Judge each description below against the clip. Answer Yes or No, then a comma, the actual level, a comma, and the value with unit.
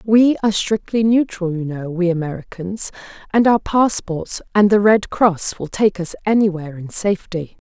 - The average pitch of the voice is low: No, high, 195 Hz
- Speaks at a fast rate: No, average, 165 wpm